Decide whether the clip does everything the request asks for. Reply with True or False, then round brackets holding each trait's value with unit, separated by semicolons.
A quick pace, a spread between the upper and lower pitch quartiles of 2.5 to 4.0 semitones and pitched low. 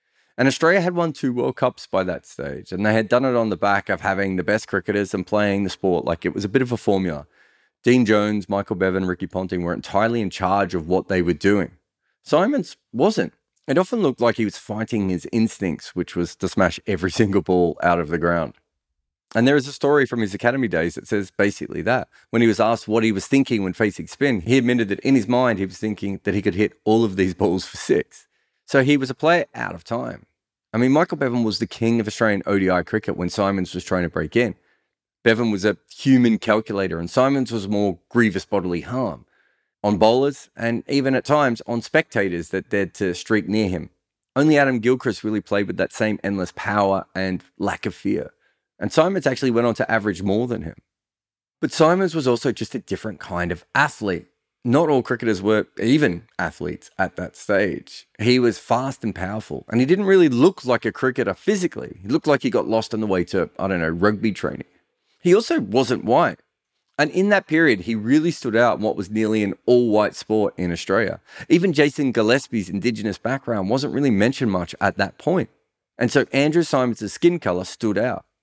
False (215 wpm; 4.5 semitones; 110 Hz)